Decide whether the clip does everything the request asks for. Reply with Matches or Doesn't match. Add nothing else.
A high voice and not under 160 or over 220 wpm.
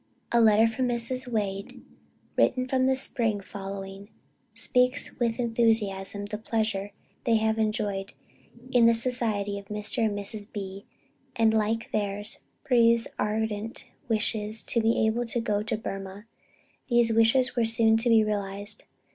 Doesn't match